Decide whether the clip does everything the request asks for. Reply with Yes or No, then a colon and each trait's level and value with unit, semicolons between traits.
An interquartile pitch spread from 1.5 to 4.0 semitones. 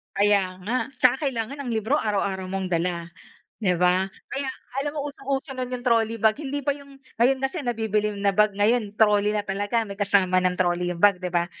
No: average, 5.0 semitones